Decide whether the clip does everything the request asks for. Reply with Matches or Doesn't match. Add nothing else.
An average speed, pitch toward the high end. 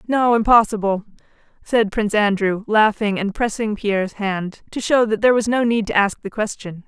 Matches